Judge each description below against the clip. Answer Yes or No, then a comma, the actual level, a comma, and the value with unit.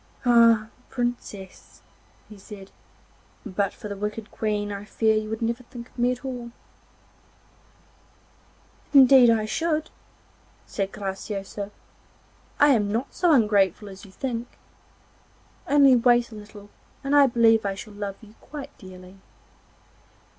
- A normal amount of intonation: Yes, average, 3.2 semitones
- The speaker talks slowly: Yes, slow, 130 wpm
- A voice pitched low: No, high, 220 Hz